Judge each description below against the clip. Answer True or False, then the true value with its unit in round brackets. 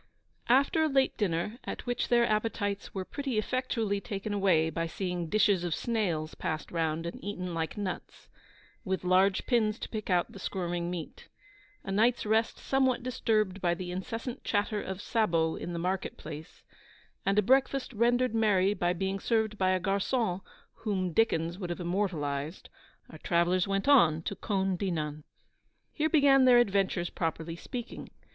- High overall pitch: True (195 Hz)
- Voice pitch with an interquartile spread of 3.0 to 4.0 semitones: False (4.4 semitones)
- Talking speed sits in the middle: True (165 wpm)